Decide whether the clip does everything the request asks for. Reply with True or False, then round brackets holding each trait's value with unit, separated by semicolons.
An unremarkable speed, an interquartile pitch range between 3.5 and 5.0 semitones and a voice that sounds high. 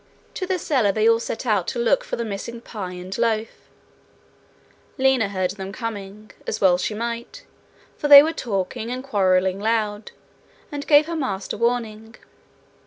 True (165 wpm; 3.8 semitones; 225 Hz)